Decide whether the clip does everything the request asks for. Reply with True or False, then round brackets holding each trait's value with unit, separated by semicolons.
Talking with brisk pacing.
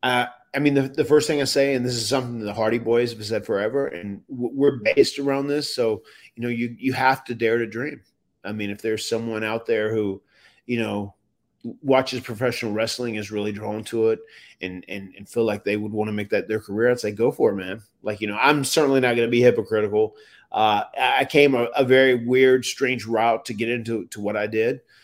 True (235 wpm)